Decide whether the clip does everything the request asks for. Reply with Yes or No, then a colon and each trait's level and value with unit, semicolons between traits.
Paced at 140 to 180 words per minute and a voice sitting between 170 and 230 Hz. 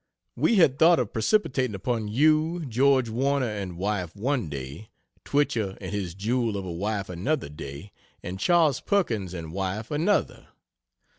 No: average, 150 wpm; low, 110 Hz